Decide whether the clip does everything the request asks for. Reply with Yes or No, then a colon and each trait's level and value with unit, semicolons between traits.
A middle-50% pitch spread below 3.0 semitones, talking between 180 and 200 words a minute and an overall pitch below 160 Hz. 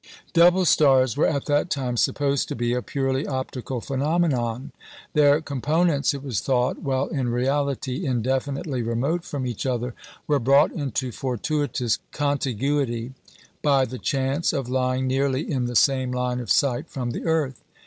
No: narrow, 2.4 semitones; average, 155 wpm; low, 135 Hz